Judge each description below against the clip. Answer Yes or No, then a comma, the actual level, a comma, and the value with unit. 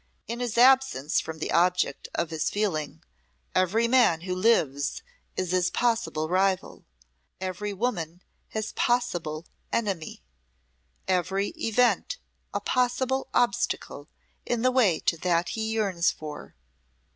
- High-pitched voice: Yes, high, 195 Hz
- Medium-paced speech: No, slow, 120 wpm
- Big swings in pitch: Yes, wide, 5.9 semitones